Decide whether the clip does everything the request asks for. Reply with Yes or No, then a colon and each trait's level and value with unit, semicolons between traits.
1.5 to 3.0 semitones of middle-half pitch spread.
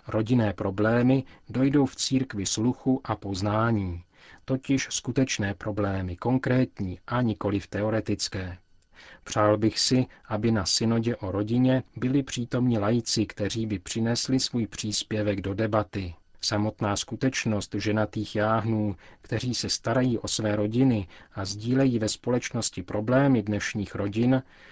No: average, 3.4 semitones